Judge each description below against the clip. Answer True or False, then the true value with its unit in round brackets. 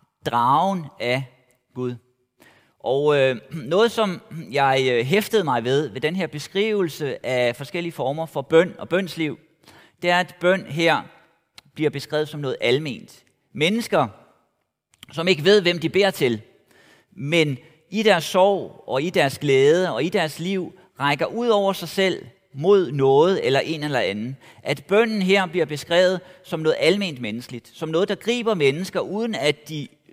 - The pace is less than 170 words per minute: True (155 wpm)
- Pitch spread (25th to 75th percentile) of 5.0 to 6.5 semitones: True (5.4 semitones)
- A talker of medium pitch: True (165 Hz)